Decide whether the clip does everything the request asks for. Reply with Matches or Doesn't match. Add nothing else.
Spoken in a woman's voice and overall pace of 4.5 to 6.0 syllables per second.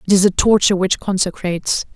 Doesn't match